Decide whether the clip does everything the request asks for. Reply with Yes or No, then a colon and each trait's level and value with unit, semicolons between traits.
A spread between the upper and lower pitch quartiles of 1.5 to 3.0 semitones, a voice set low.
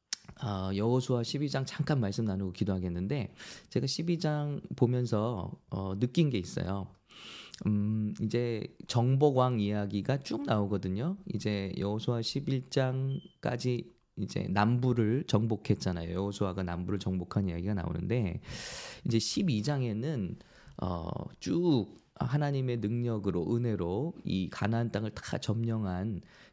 No: average, 4.2 semitones; low, 110 Hz